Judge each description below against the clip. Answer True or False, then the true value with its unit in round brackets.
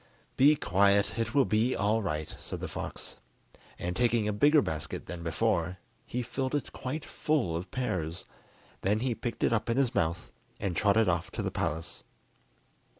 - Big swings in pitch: True (5.9 semitones)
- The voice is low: True (105 Hz)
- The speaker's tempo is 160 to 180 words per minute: True (175 wpm)